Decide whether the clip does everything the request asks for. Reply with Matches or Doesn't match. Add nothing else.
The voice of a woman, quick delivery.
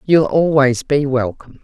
Doesn't match